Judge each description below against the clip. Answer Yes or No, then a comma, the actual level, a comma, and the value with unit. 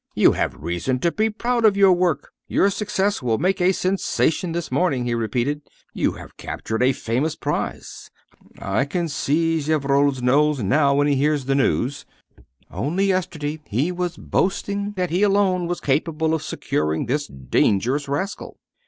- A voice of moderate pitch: Yes, medium, 150 Hz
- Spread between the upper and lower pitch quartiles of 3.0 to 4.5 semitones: No, average, 5.3 semitones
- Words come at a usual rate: Yes, average, 160 wpm